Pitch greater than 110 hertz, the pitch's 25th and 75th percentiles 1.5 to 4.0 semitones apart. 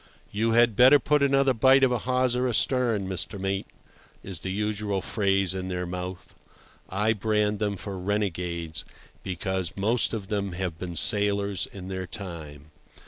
No: low, 100 Hz; average, 3.3 semitones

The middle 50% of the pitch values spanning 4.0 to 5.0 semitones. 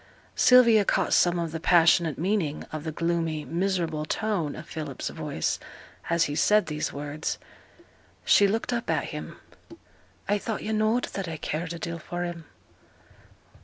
Yes: average, 4.4 semitones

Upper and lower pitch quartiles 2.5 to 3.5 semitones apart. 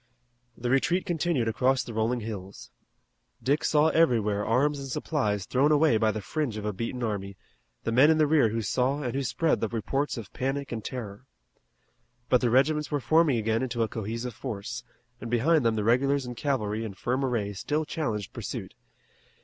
No: average, 4.3 semitones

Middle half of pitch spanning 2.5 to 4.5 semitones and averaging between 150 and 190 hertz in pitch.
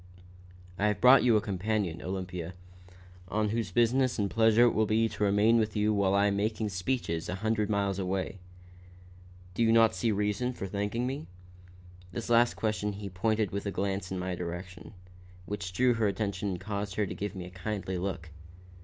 No: average, 2.8 semitones; low, 105 Hz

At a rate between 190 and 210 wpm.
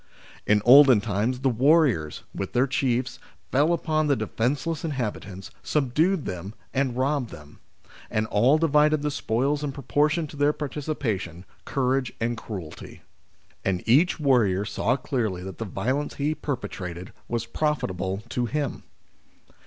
No: slow, 135 wpm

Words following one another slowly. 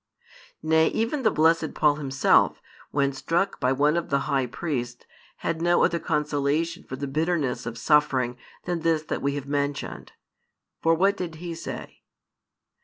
No: average, 160 wpm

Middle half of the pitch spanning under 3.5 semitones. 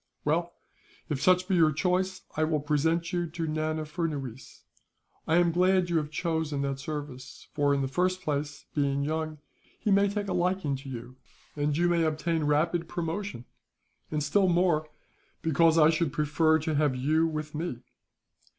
Yes: average, 2.8 semitones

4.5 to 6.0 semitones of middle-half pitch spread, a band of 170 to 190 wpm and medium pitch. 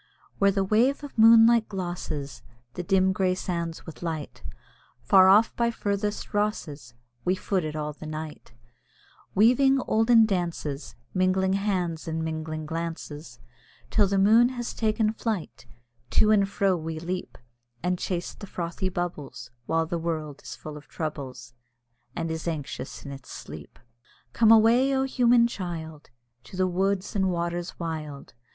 No: average, 4.8 semitones; average, 150 wpm; medium, 180 Hz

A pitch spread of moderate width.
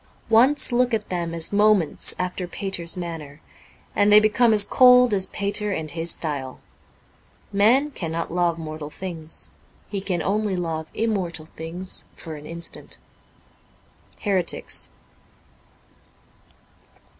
Yes: average, 4.2 semitones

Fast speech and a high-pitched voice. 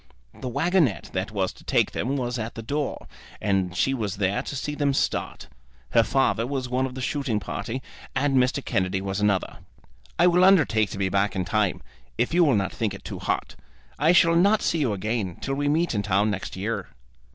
No: fast, 210 wpm; low, 120 Hz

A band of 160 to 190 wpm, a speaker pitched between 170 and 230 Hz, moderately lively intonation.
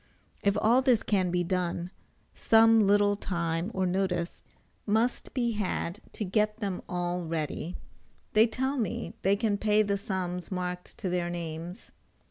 No: average, 150 wpm; high, 190 Hz; average, 3.2 semitones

